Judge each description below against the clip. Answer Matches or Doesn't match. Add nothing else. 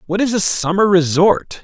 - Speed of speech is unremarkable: Matches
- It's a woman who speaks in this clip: Doesn't match